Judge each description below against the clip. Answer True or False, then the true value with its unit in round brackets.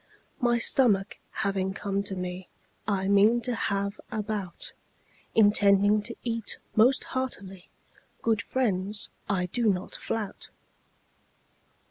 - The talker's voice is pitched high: True (205 Hz)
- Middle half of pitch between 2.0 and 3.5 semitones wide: True (2.7 semitones)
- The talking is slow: True (115 wpm)